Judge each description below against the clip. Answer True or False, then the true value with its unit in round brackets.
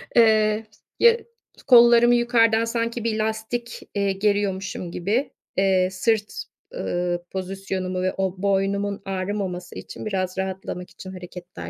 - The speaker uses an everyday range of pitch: True (3.2 semitones)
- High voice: True (200 Hz)